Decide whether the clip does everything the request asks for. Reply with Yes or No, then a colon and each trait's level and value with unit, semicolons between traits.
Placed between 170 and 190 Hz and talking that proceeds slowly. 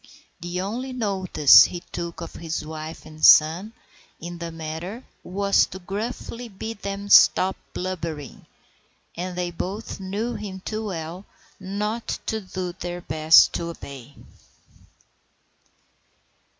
Yes: medium, 185 Hz; slow, 125 wpm